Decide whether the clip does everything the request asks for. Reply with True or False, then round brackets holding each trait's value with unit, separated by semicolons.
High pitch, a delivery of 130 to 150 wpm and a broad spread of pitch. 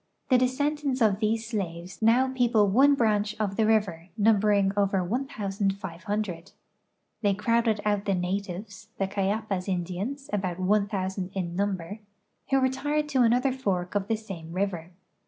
False (205 Hz; 145 wpm; 3.2 semitones)